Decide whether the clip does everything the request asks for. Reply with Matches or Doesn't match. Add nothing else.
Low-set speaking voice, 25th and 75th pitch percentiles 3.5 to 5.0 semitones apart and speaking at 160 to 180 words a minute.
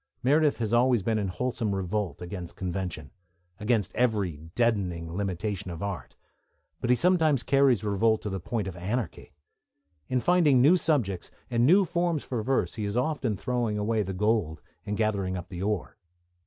Matches